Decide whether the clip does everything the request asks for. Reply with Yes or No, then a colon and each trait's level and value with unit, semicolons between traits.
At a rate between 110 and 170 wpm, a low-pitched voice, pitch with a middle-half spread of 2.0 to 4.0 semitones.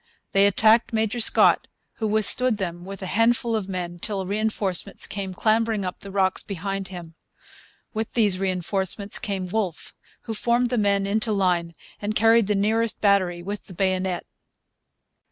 No: average, 155 wpm; high, 200 Hz; average, 2.7 semitones